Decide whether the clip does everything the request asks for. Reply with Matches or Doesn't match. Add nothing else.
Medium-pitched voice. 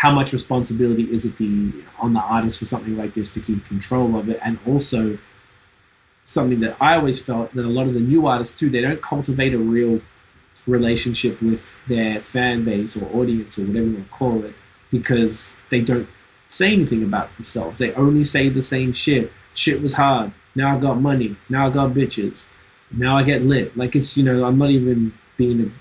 Doesn't match